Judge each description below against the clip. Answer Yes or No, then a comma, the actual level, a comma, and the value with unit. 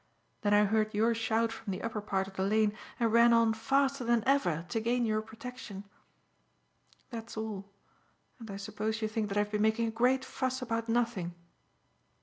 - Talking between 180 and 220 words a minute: Yes, average, 190 wpm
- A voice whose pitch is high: Yes, high, 220 Hz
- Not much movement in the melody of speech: Yes, narrow, 1.9 semitones